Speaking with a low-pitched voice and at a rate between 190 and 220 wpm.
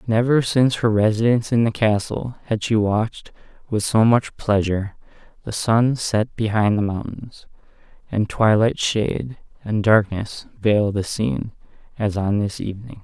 No: low, 110 Hz; average, 145 wpm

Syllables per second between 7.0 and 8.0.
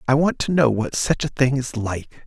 No: 4.8 syllables/s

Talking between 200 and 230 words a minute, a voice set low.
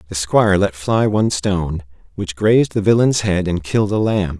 Yes: fast, 205 wpm; very low, 95 Hz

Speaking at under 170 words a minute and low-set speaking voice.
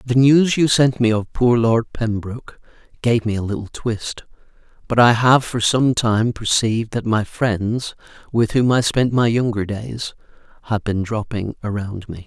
No: average, 175 wpm; low, 115 Hz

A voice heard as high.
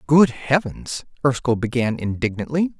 No: low, 135 Hz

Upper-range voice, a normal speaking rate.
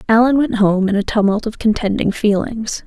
Yes: high, 215 Hz; average, 190 wpm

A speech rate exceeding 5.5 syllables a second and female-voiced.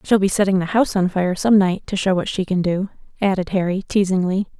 Yes: 5.9 syllables/s; female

